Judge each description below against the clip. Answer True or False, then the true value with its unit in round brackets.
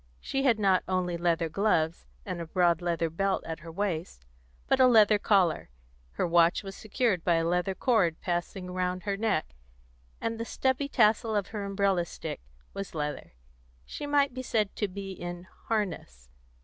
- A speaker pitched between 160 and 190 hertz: True (185 Hz)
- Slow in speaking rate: False (175 wpm)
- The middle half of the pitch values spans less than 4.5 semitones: True (3.9 semitones)